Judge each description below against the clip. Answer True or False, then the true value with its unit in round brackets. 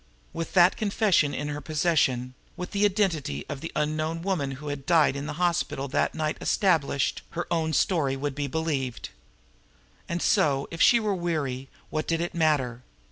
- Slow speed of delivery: False (175 wpm)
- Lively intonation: False (3.6 semitones)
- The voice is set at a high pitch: False (155 Hz)